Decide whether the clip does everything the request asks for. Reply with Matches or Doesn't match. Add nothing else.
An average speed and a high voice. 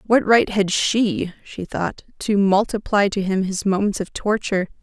Matches